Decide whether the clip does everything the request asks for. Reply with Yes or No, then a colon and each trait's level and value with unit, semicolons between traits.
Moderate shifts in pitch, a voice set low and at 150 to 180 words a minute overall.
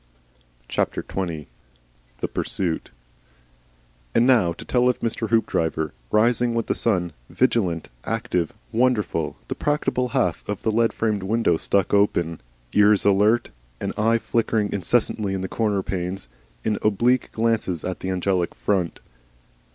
No: average, 4.0 semitones; low, 105 Hz; slow, 135 wpm